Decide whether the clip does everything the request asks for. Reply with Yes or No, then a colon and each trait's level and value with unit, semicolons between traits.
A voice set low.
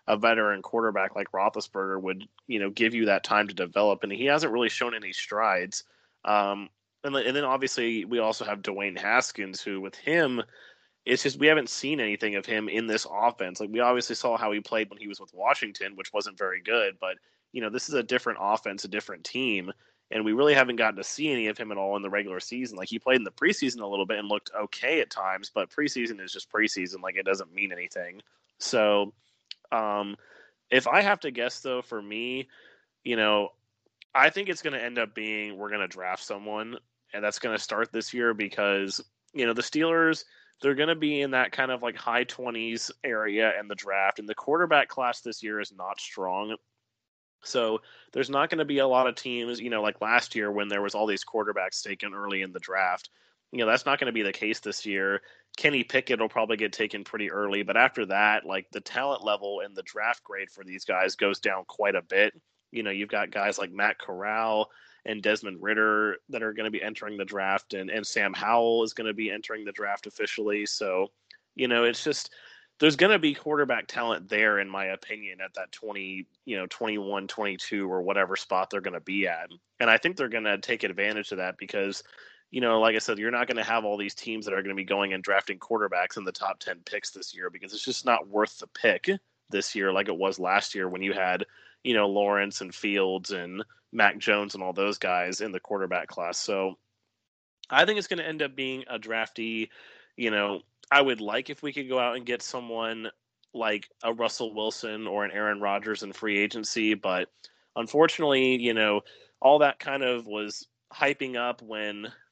Yes: low, 110 Hz